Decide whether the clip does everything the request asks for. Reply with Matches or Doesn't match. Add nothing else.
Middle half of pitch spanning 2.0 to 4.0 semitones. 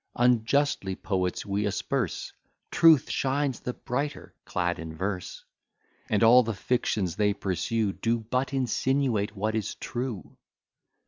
Doesn't match